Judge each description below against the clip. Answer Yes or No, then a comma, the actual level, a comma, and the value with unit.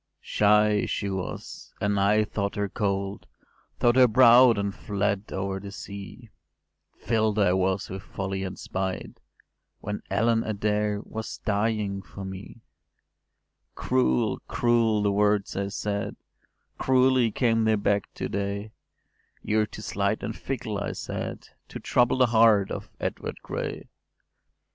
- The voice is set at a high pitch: No, low, 105 Hz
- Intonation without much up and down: Yes, narrow, 1.9 semitones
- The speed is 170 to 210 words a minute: No, slow, 135 wpm